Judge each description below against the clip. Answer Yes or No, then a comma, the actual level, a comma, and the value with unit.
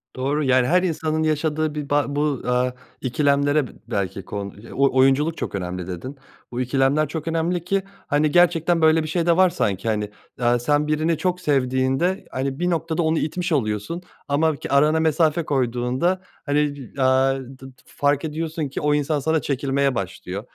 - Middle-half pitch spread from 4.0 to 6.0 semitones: No, average, 3.5 semitones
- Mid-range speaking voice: Yes, medium, 145 Hz